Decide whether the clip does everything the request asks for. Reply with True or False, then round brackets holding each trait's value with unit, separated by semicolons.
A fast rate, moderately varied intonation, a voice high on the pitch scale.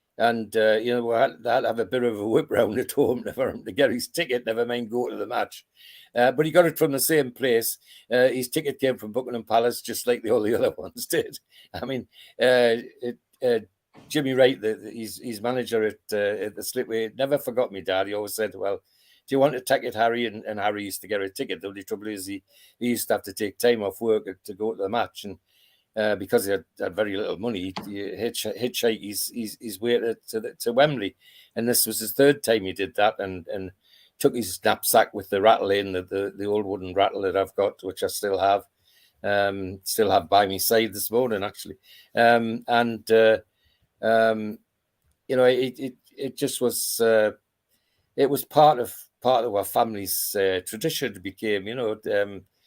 False (220 wpm; 3.4 semitones; 115 Hz)